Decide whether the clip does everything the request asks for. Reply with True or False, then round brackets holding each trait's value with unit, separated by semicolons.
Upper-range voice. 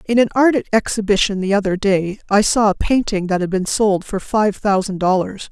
True (200 Hz)